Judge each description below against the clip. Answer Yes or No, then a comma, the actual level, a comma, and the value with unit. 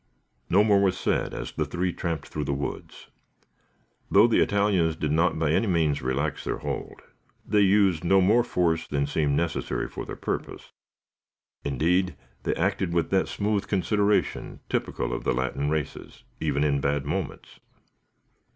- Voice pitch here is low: Yes, very low, 85 Hz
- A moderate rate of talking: Yes, average, 160 wpm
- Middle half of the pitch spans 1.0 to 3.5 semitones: No, average, 5.0 semitones